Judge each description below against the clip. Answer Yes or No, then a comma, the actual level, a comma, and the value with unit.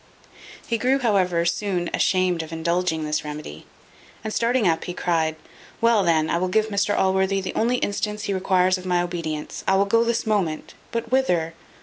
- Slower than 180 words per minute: No, average, 185 wpm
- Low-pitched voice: No, medium, 185 Hz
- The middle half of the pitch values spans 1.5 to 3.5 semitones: No, average, 4.0 semitones